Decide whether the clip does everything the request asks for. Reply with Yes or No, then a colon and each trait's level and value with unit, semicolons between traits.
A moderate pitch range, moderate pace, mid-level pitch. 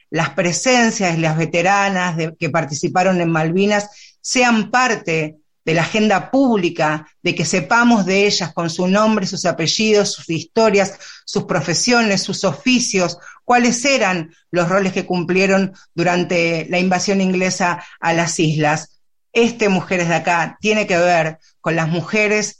Yes: average, 3.6 semitones; average, 145 wpm; medium, 180 Hz